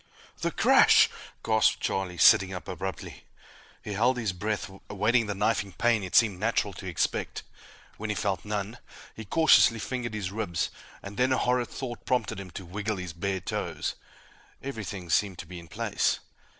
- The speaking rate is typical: Yes, average, 170 wpm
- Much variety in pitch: No, average, 3.2 semitones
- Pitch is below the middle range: Yes, low, 105 Hz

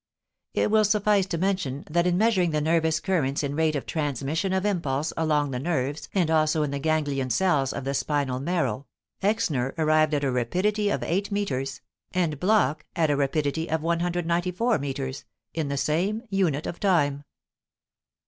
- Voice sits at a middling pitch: Yes, medium, 155 Hz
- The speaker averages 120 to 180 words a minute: Yes, average, 170 wpm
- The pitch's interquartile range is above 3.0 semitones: Yes, average, 4.4 semitones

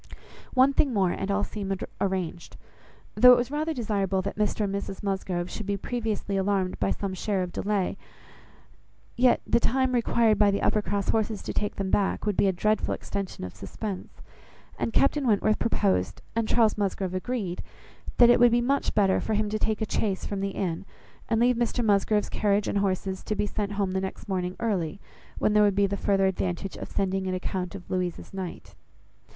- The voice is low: No, high, 200 Hz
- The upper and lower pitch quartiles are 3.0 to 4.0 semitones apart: No, narrow, 2.5 semitones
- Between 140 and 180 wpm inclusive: No, average, 200 wpm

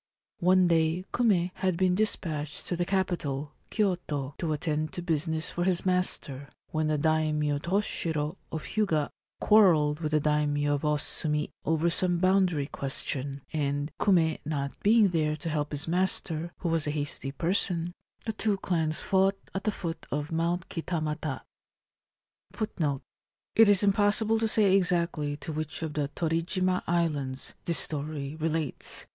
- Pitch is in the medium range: Yes, medium, 160 Hz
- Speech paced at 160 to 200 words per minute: No, average, 150 wpm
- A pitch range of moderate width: Yes, average, 3.5 semitones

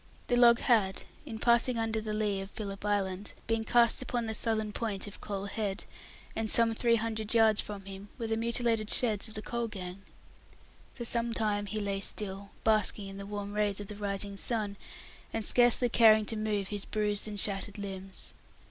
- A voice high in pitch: Yes, high, 215 Hz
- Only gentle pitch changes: Yes, narrow, 2.1 semitones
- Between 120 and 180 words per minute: No, average, 190 wpm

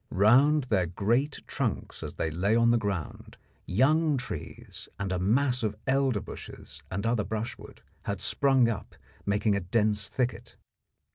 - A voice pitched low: Yes, low, 110 Hz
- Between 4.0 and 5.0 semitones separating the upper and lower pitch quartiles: Yes, average, 4.4 semitones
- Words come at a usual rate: Yes, average, 150 wpm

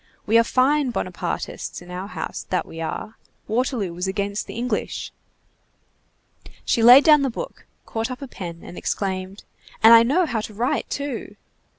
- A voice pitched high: Yes, high, 230 Hz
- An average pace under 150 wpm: No, average, 170 wpm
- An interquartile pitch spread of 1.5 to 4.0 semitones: No, average, 4.9 semitones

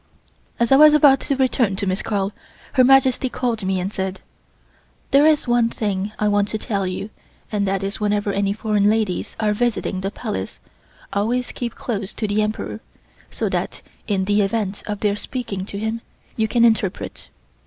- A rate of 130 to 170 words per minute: No, average, 185 wpm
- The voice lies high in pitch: Yes, high, 210 Hz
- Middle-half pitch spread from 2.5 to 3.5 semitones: Yes, average, 3.1 semitones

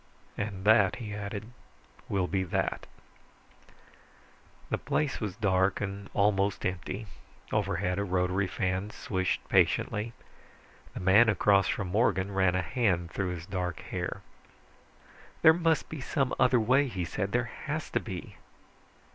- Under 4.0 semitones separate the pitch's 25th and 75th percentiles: Yes, average, 3.0 semitones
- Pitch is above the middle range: No, low, 100 Hz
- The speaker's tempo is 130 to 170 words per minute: Yes, average, 140 wpm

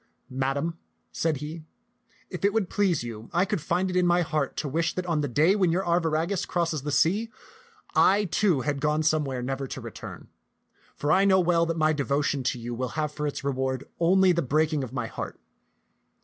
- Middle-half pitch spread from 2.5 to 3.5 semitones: No, average, 4.1 semitones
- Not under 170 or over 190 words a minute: No, fast, 205 wpm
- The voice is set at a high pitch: No, medium, 155 Hz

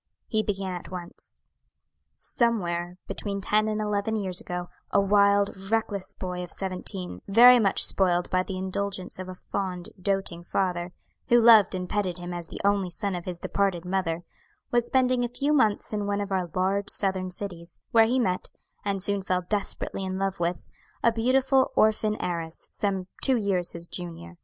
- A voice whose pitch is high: Yes, high, 195 Hz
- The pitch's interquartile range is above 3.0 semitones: No, average, 2.7 semitones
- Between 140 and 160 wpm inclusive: No, average, 175 wpm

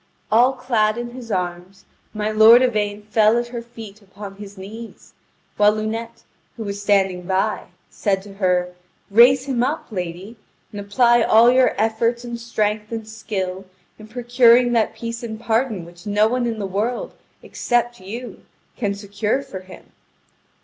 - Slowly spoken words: No, average, 160 wpm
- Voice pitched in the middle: No, high, 220 Hz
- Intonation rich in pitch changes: No, average, 2.9 semitones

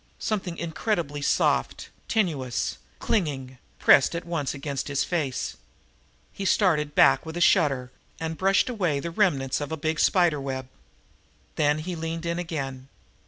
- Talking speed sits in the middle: Yes, average, 145 wpm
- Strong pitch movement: No, average, 3.8 semitones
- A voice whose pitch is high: No, medium, 160 Hz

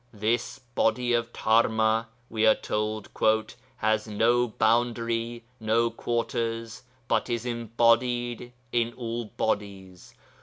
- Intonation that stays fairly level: Yes, narrow, 1.4 semitones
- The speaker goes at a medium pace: No, slow, 105 wpm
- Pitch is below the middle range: Yes, low, 115 Hz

